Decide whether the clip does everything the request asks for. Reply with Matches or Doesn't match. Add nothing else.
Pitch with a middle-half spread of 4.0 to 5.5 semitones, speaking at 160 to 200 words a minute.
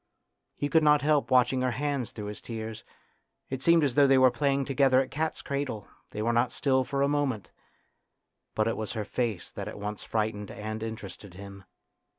Matches